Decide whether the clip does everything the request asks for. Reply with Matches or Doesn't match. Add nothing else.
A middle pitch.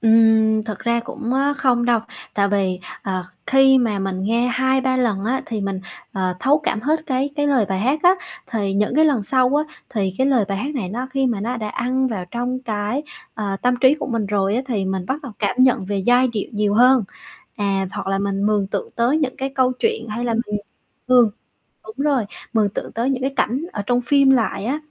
Doesn't match